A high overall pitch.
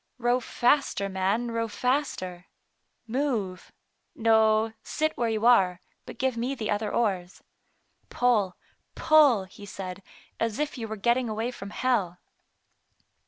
Yes: high, 225 Hz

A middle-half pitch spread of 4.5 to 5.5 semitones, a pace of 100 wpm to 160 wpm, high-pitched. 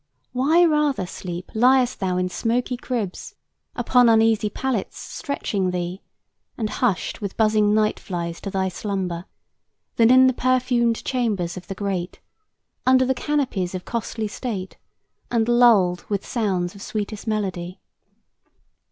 Yes: average, 4.8 semitones; slow, 135 wpm; high, 215 Hz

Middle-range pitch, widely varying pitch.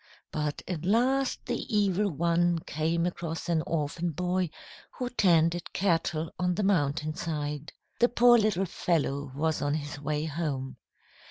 No: medium, 165 Hz; average, 3.5 semitones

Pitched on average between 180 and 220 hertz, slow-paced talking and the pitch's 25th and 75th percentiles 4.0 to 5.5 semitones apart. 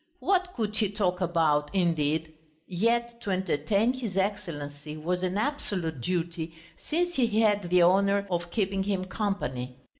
No: medium, 185 Hz; average, 145 wpm; average, 4.3 semitones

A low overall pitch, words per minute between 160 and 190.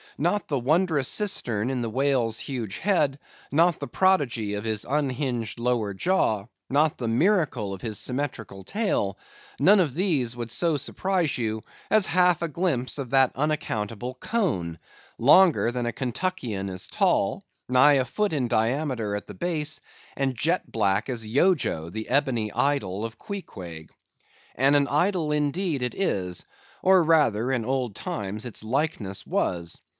No: low, 130 Hz; average, 150 wpm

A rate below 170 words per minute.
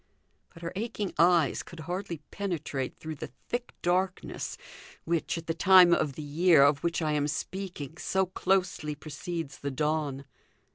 Yes: average, 155 wpm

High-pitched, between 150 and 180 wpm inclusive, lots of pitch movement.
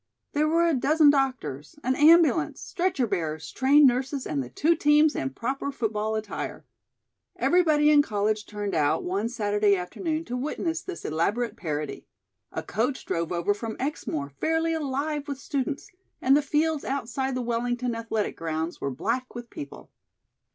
Yes: very high, 250 Hz; average, 160 wpm; wide, 6.5 semitones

